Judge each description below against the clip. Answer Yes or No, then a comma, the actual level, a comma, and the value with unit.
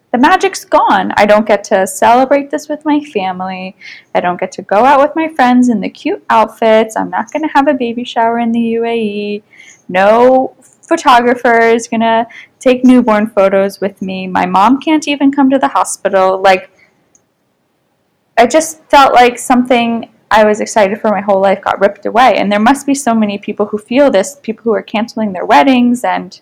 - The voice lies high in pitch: Yes, high, 230 Hz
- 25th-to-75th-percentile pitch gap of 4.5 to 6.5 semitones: Yes, average, 4.8 semitones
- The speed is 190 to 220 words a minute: Yes, average, 200 wpm